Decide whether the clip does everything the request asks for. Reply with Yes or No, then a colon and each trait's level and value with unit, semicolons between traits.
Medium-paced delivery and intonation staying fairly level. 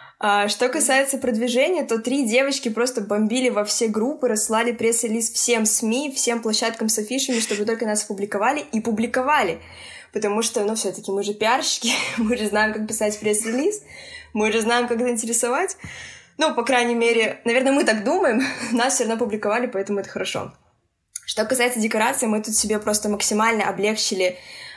No: fast, 165 wpm; narrow, 2.3 semitones